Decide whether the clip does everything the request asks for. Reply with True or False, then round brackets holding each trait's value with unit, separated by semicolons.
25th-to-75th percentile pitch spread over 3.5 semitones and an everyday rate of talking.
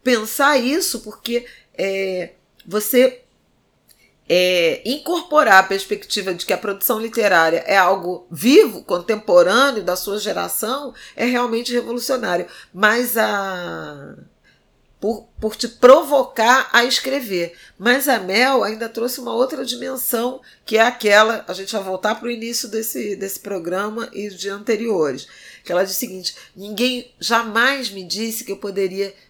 True (4.1 semitones; 140 wpm)